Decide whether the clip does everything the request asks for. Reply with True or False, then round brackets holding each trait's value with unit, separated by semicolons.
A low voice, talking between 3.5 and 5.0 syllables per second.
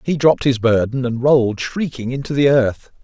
False (130 Hz; 5.3 syllables/s)